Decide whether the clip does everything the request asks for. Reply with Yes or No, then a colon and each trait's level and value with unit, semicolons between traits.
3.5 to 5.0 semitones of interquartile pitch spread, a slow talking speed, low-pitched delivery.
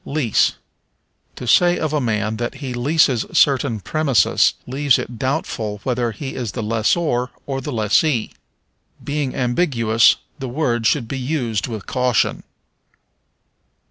Yes: average, 3.8 semitones; slow, 125 wpm; low, 125 Hz